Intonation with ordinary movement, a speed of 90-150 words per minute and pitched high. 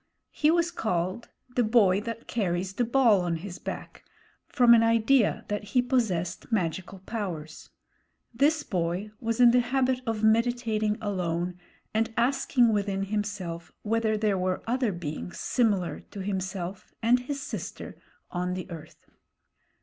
Yes: average, 4.3 semitones; average, 140 wpm; high, 210 Hz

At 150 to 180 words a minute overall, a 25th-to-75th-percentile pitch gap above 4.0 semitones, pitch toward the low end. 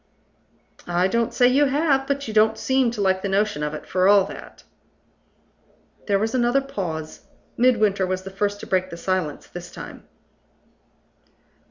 No: average, 165 wpm; average, 4.7 semitones; high, 205 Hz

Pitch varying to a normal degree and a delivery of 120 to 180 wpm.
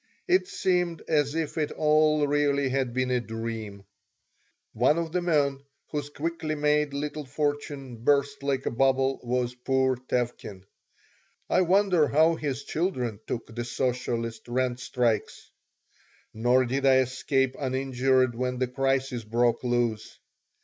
Yes: average, 3.2 semitones; slow, 135 wpm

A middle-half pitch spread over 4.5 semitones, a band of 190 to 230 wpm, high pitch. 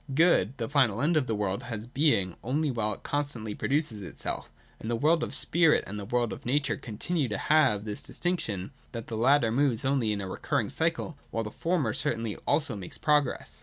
No: wide, 5.5 semitones; fast, 205 wpm; low, 120 Hz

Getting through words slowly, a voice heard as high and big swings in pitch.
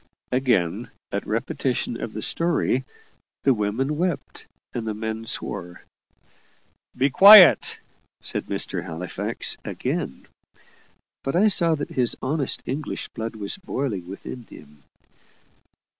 No: slow, 115 wpm; low, 125 Hz; wide, 6.4 semitones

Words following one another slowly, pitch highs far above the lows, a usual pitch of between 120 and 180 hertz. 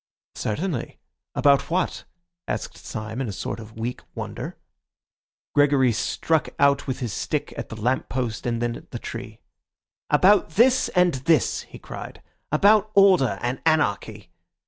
No: average, 145 wpm; wide, 5.7 semitones; low, 135 Hz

